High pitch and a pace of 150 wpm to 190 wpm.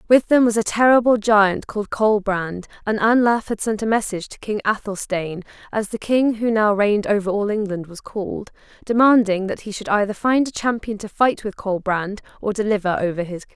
No: high, 210 Hz; average, 200 wpm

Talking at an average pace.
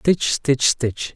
Yes: average, 155 wpm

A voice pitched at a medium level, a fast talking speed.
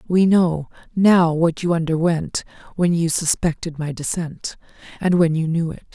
No: medium, 165 Hz; average, 160 wpm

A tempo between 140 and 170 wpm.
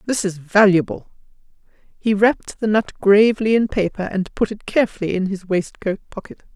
Yes: average, 165 wpm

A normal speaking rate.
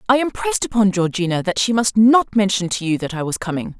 No: fast, 235 wpm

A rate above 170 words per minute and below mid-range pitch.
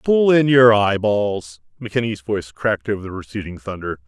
No: average, 160 wpm; low, 105 Hz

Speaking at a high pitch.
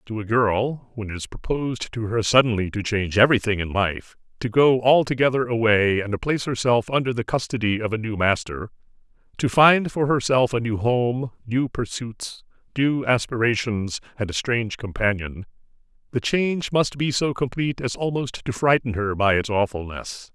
No: low, 115 Hz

